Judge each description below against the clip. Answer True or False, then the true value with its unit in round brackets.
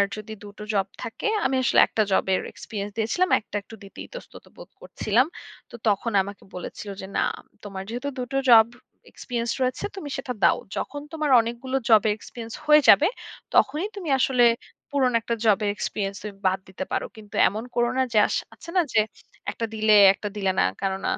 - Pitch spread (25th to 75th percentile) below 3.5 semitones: False (4.0 semitones)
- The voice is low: False (225 Hz)